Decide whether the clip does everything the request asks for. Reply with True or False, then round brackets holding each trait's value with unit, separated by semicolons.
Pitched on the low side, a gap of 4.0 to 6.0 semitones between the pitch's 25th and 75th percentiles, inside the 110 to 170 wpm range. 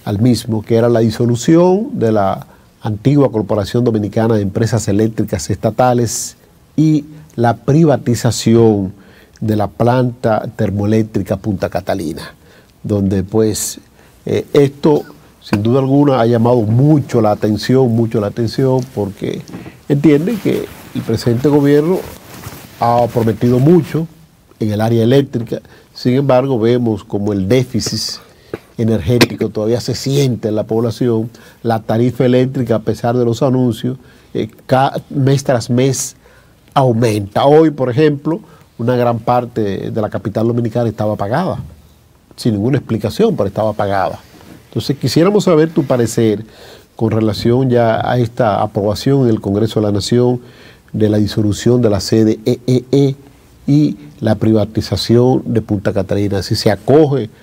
False (115 Hz; 3.1 semitones; 135 wpm)